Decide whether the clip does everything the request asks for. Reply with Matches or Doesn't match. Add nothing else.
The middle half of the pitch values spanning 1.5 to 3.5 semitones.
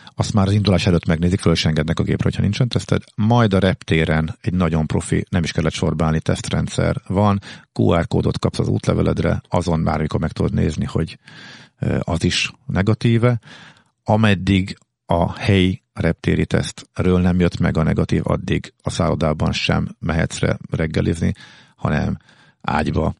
Doesn't match